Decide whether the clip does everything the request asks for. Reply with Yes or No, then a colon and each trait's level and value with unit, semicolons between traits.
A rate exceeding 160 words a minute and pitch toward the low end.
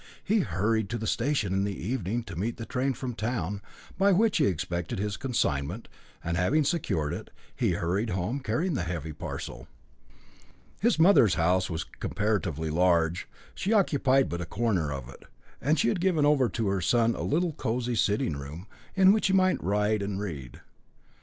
Yes: average, 180 wpm; low, 105 Hz